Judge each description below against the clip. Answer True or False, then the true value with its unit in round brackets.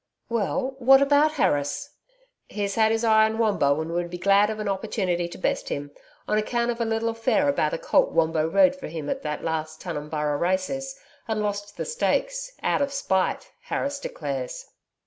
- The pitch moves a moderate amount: False (8.3 semitones)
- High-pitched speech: True (210 Hz)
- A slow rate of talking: False (185 wpm)